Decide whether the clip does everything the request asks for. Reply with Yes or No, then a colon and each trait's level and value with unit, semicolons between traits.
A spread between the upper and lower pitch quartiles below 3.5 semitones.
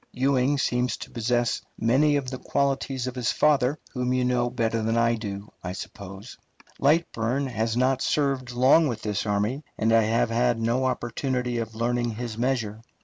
Yes: narrow, 2.5 semitones